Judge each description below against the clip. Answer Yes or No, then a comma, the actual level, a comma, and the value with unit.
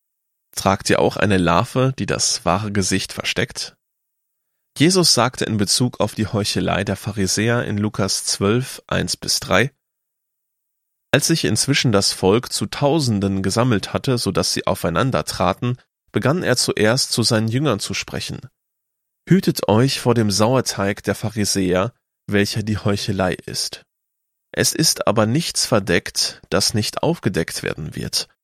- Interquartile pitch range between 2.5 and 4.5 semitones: Yes, average, 3.9 semitones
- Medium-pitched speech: No, low, 105 Hz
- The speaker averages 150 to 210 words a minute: No, average, 140 wpm